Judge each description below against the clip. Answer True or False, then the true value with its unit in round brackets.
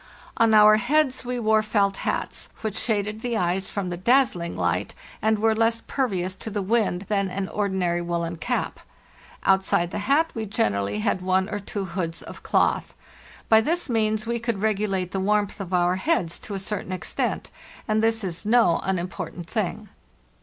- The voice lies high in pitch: True (205 Hz)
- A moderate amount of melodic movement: True (3.3 semitones)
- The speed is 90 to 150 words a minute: False (175 wpm)